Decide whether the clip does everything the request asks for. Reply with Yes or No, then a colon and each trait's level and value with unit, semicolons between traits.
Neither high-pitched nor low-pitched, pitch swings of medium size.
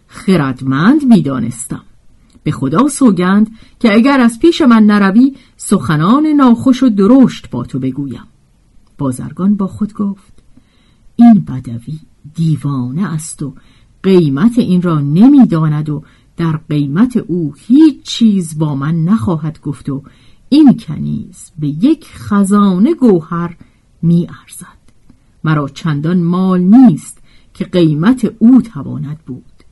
No: medium, 175 Hz; wide, 7.9 semitones